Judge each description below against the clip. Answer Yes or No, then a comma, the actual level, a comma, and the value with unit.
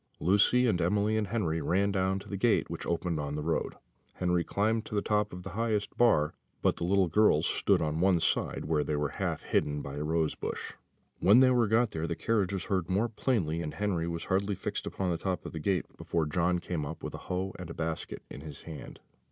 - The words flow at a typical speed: No, fast, 235 wpm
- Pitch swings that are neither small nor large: Yes, average, 4.0 semitones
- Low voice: Yes, very low, 90 Hz